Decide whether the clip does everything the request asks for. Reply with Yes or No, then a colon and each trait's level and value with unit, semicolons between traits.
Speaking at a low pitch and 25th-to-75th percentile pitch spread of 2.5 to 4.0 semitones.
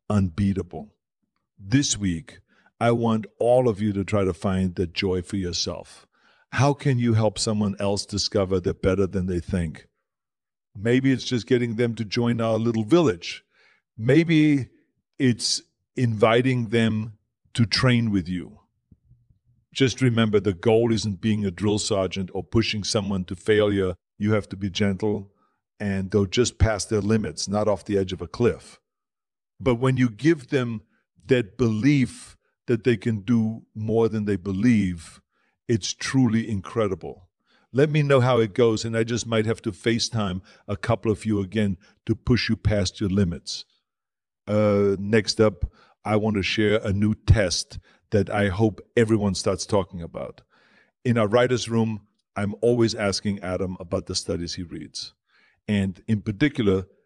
Yes: low, 110 Hz; average, 3.0 semitones